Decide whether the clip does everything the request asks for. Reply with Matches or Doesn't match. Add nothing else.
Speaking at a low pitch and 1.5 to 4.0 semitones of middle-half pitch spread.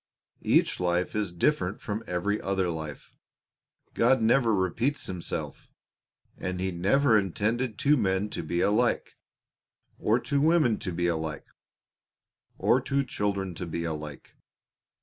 Doesn't match